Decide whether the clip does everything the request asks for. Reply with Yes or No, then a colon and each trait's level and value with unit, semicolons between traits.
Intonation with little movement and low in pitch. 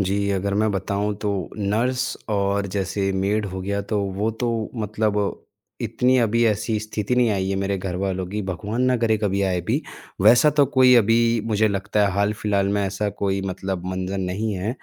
Yes: narrow, 2.1 semitones; low, 100 Hz